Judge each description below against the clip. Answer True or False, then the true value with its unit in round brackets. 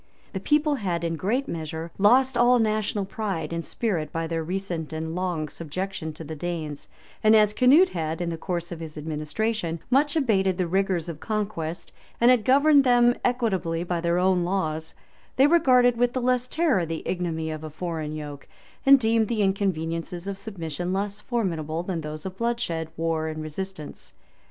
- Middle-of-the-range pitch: True (180 Hz)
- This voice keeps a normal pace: True (180 wpm)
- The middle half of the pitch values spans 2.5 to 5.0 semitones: False (5.5 semitones)